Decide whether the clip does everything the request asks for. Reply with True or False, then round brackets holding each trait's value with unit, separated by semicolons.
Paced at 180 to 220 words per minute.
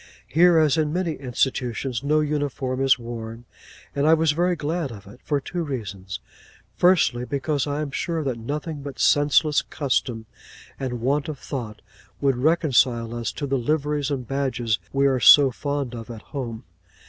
False (170 wpm)